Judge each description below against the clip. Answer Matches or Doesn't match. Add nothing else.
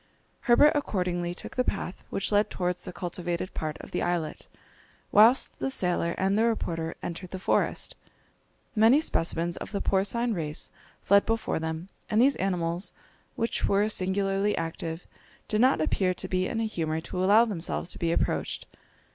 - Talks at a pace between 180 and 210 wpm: Doesn't match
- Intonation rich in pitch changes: Doesn't match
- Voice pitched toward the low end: Doesn't match